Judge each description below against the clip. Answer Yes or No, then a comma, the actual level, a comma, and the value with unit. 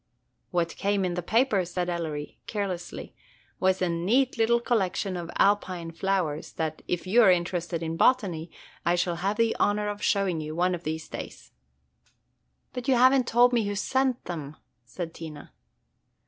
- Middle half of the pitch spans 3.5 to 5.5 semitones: Yes, average, 3.8 semitones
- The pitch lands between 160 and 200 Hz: Yes, medium, 185 Hz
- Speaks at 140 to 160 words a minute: No, average, 170 wpm